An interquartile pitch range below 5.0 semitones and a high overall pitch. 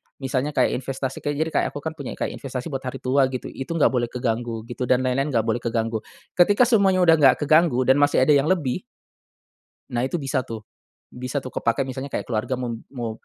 No: average, 2.9 semitones; low, 130 Hz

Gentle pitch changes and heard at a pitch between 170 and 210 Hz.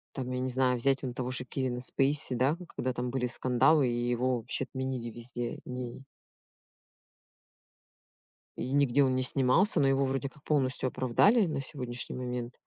No: narrow, 1.6 semitones; low, 130 Hz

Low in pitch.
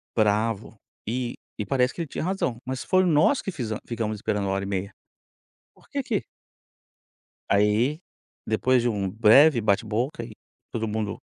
Yes: low, 115 Hz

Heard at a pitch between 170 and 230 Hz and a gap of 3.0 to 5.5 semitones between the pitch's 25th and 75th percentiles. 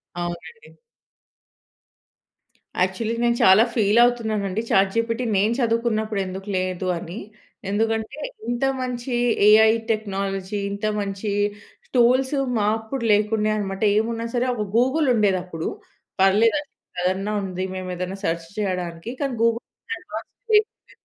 Yes: high, 215 Hz; average, 3.3 semitones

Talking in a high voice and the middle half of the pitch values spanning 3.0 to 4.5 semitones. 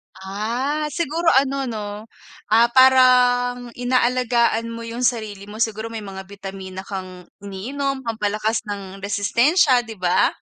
Yes: high, 230 Hz; average, 3.9 semitones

